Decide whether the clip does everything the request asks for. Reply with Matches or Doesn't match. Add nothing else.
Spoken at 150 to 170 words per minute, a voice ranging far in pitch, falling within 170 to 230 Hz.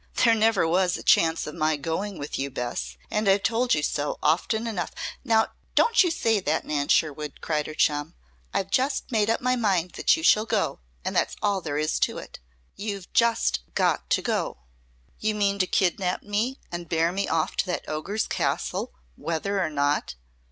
Doesn't match